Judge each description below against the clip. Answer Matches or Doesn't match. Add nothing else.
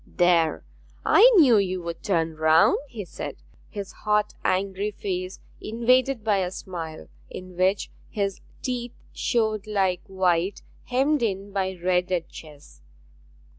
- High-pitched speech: Matches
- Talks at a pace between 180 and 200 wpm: Doesn't match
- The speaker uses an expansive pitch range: Doesn't match